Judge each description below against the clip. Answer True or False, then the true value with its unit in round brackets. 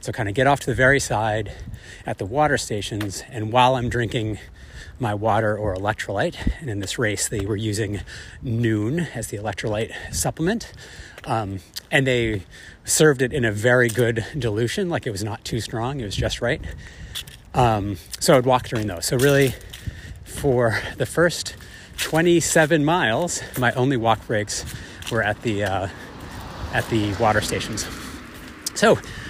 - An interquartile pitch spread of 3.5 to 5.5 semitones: True (3.8 semitones)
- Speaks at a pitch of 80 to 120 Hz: True (110 Hz)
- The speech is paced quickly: False (160 wpm)